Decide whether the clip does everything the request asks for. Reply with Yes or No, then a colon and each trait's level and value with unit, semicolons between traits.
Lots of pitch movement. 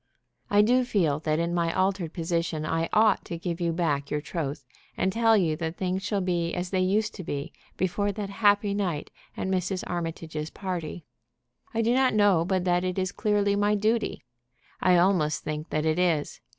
No: average, 3.7 semitones